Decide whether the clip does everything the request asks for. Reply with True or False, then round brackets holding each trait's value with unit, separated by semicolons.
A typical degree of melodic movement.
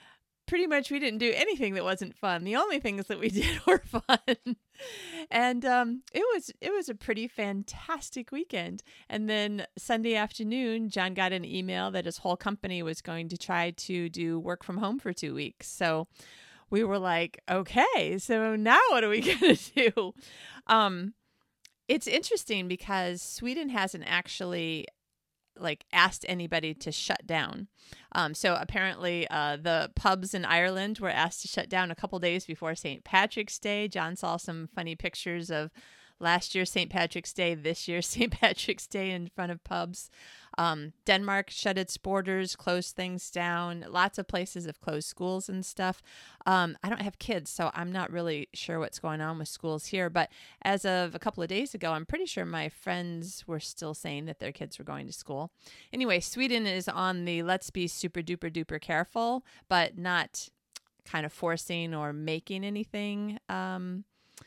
True (4.0 semitones)